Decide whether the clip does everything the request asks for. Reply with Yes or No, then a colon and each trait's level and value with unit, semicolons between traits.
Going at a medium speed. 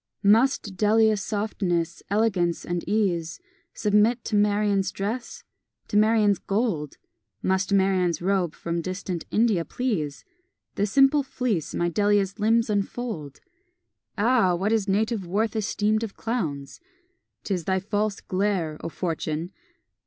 No: slow, 125 wpm